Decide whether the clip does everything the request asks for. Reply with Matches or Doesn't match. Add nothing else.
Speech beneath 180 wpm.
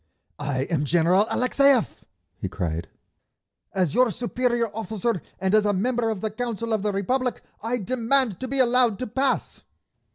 Matches